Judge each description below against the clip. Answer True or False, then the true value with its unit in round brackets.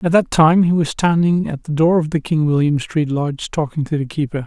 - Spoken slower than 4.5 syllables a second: False (5.5 syllables/s)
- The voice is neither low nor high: True (155 Hz)